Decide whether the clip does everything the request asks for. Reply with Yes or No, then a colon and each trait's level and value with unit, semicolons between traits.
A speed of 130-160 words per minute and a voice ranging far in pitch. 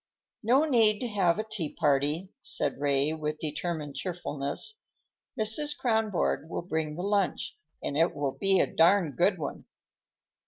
Yes: average, 150 wpm; wide, 5.9 semitones